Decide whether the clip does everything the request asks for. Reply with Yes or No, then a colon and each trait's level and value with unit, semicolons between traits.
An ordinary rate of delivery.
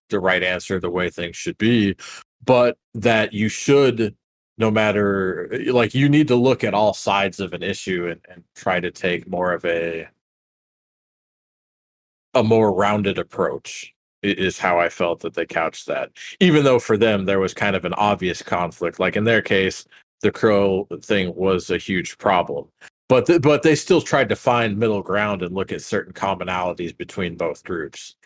Yes: average, 180 wpm